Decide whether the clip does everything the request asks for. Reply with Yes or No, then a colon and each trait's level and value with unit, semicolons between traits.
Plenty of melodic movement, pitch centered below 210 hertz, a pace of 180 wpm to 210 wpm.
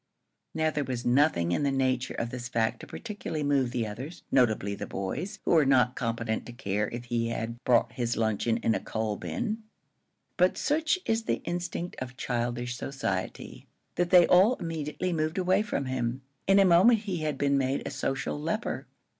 Yes: wide, 6.4 semitones; low, 135 Hz; average, 190 wpm